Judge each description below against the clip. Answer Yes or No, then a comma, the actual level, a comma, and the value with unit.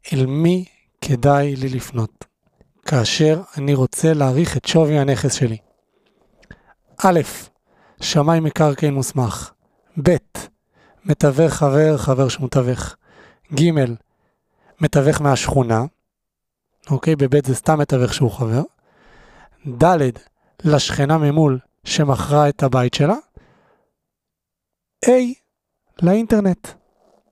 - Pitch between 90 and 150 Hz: Yes, medium, 140 Hz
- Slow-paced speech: Yes, slow, 95 wpm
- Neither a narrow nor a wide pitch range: Yes, average, 3.2 semitones